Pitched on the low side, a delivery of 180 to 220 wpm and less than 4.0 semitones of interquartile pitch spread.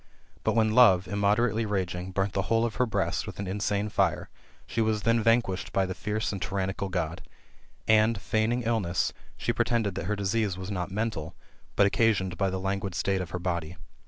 Yes: low, 100 Hz; average, 195 wpm; average, 2.9 semitones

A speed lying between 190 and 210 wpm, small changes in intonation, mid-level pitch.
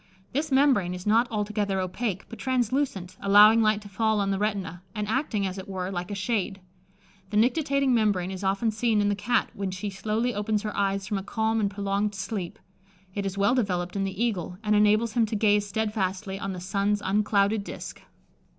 No: average, 200 wpm; narrow, 2.2 semitones; high, 205 Hz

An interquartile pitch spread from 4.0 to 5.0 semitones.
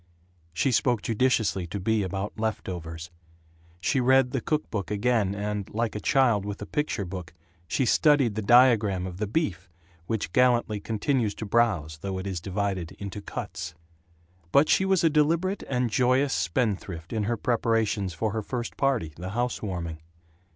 Yes: average, 4.7 semitones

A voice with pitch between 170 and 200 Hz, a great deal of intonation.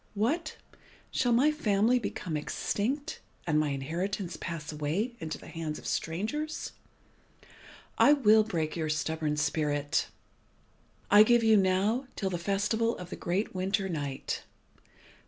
Yes: high, 190 Hz; wide, 6.1 semitones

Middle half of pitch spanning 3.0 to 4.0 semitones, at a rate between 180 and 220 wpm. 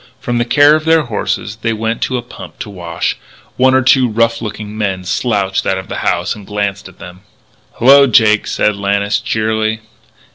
Yes: average, 3.3 semitones; average, 190 wpm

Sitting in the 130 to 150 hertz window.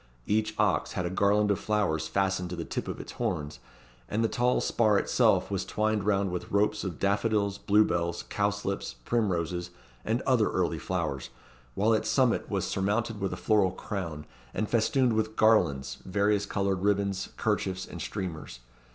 No: low, 100 Hz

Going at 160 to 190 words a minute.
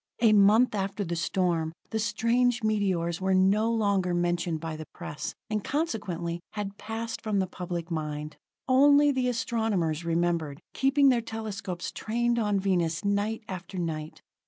No: average, 150 wpm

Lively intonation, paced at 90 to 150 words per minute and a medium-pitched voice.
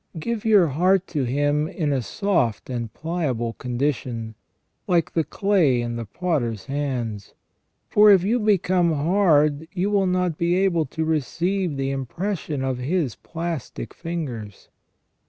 Yes: wide, 5.9 semitones; average, 145 wpm; medium, 155 Hz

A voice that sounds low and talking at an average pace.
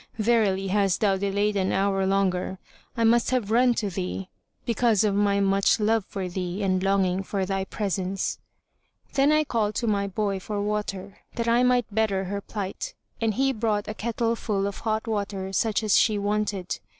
No: high, 205 Hz; average, 185 wpm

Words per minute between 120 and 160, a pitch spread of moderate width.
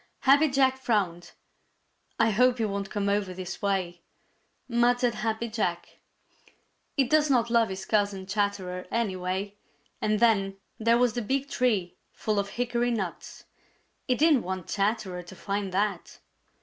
Yes: average, 145 wpm; average, 3.9 semitones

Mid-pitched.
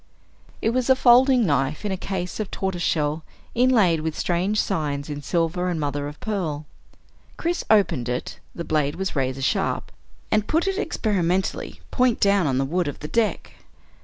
Yes: medium, 180 Hz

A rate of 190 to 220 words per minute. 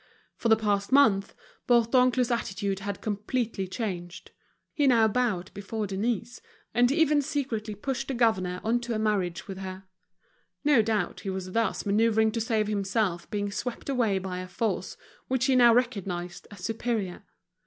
No: average, 160 wpm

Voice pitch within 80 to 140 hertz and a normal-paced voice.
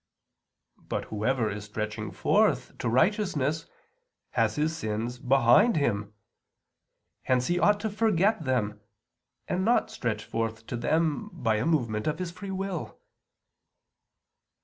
No: low, 135 Hz; slow, 125 wpm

